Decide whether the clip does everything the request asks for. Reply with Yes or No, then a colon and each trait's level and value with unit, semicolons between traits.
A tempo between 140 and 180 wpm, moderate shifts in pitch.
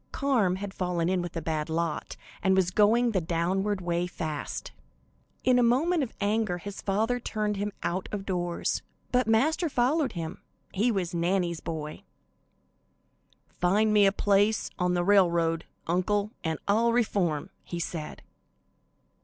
Yes: average, 150 wpm; average, 4.1 semitones